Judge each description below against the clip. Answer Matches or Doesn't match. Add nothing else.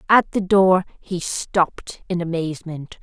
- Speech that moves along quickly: Doesn't match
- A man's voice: Doesn't match